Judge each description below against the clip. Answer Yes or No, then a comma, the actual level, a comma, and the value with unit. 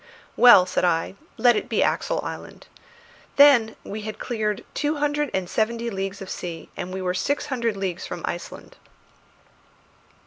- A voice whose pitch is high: Yes, high, 215 Hz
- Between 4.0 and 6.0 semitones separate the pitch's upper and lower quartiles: Yes, average, 4.8 semitones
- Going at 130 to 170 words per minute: Yes, average, 160 wpm